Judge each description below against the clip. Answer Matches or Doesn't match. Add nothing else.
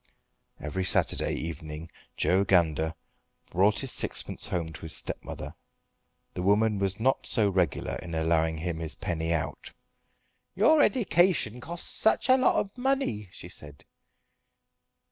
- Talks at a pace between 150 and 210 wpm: Doesn't match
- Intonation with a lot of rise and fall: Matches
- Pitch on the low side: Matches